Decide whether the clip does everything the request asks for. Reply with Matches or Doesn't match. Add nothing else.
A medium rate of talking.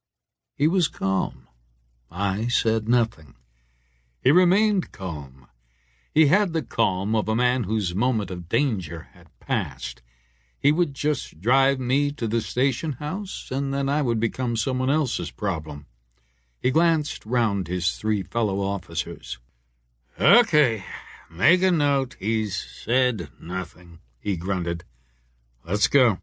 Doesn't match